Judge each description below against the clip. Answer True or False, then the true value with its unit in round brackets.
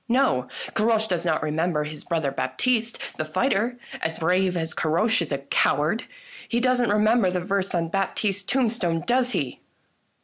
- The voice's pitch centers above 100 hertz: True (185 Hz)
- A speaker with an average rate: True (165 wpm)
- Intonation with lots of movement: True (5.8 semitones)